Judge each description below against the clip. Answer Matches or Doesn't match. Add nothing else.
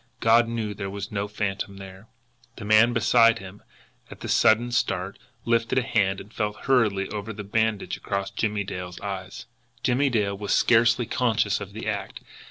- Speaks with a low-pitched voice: Matches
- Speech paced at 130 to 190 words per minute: Matches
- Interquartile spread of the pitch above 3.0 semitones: Doesn't match